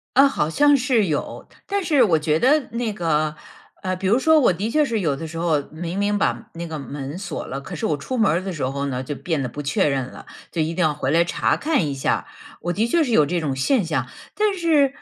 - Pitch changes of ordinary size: No, wide, 8.1 semitones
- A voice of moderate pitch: Yes, medium, 175 Hz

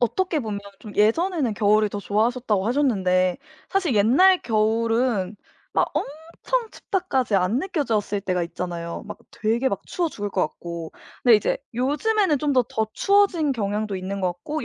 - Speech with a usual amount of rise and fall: No, wide, 6.6 semitones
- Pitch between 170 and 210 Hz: No, high, 225 Hz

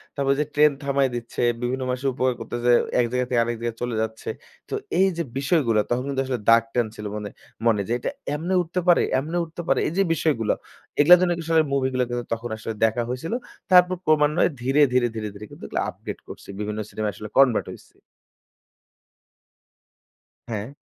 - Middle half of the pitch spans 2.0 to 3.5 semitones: No, average, 4.4 semitones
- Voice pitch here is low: Yes, low, 125 Hz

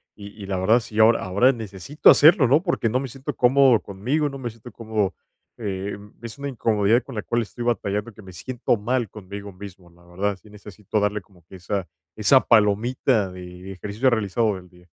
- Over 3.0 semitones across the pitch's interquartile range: Yes, average, 3.7 semitones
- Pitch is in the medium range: No, low, 105 Hz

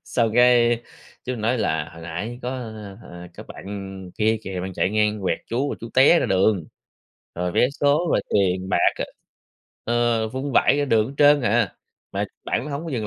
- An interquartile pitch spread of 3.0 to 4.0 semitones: No, average, 4.5 semitones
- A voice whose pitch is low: Yes, low, 110 Hz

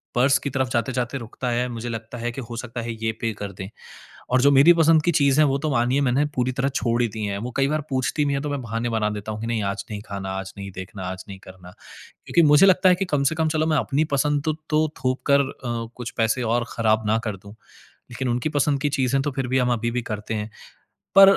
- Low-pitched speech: Yes, low, 125 Hz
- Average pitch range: Yes, average, 4.0 semitones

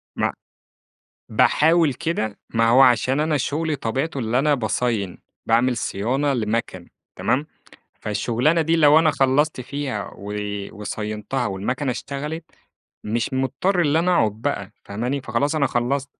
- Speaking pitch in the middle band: No, low, 130 Hz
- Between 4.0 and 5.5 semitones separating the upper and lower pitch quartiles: Yes, average, 4.7 semitones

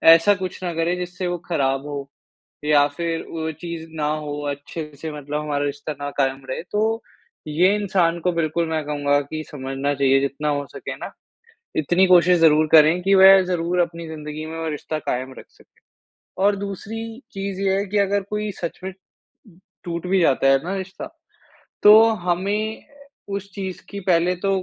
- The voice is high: No, medium, 165 Hz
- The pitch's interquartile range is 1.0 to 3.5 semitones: No, average, 4.2 semitones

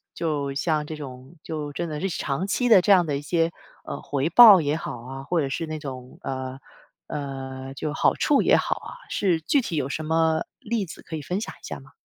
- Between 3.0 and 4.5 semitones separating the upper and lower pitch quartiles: Yes, average, 3.9 semitones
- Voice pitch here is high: No, medium, 155 Hz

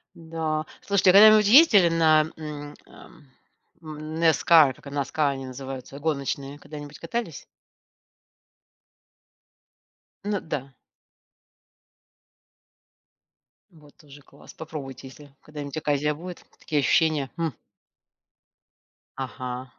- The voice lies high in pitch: No, medium, 150 Hz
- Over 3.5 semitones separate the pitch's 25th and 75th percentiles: No, average, 2.8 semitones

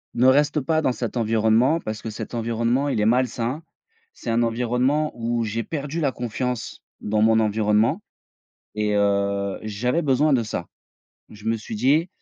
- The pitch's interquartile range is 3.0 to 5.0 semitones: Yes, average, 3.3 semitones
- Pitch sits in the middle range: No, low, 115 Hz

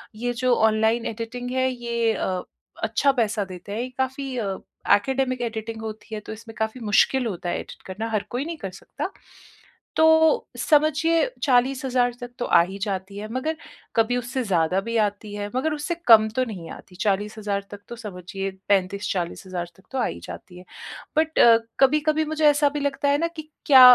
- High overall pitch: Yes, high, 230 Hz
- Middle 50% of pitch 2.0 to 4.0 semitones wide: No, average, 4.7 semitones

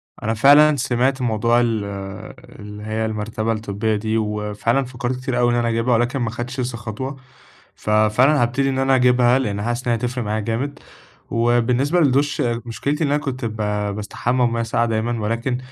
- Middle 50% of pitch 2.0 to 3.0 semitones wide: Yes, average, 2.7 semitones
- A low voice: Yes, low, 120 Hz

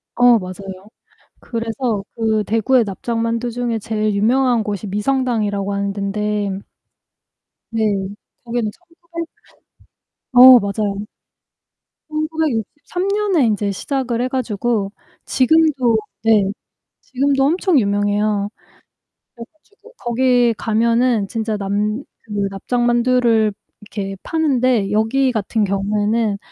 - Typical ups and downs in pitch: Yes, average, 3.5 semitones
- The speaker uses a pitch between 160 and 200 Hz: No, high, 230 Hz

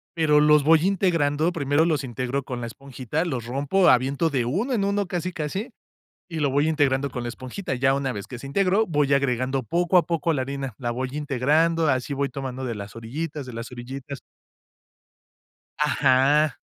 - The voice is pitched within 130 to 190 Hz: Yes, medium, 140 Hz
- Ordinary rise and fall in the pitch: Yes, average, 3.9 semitones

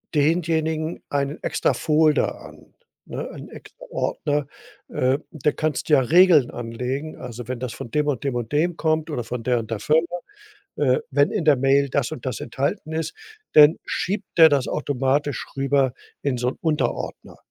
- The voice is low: No, medium, 145 Hz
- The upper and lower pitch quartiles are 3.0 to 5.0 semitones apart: Yes, average, 3.6 semitones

